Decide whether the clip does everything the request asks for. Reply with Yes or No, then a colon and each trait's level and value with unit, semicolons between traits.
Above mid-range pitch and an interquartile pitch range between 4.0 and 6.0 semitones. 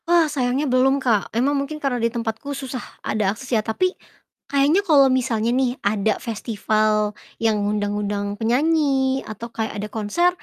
Yes: high, 245 Hz; average, 4.3 semitones